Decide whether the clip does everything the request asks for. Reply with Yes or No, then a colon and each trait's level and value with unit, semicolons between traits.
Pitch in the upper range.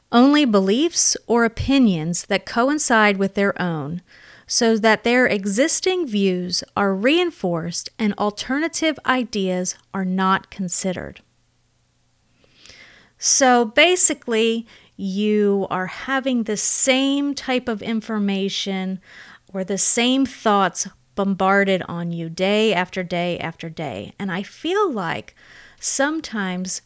Yes: high, 205 Hz